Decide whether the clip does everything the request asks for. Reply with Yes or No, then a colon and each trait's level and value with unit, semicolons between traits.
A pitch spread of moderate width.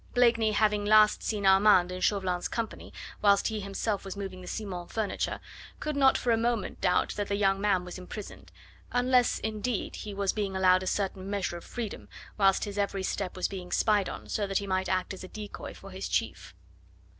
No: narrow, 2.3 semitones